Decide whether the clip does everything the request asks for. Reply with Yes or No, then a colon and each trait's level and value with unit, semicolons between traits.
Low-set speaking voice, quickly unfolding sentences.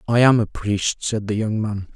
Yes: low, 110 Hz; fast, 245 wpm